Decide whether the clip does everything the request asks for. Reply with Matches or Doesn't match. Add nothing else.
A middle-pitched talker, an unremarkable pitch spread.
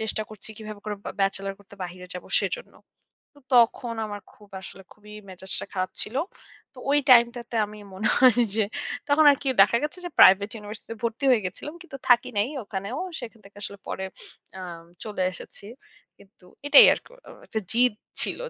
Doesn't match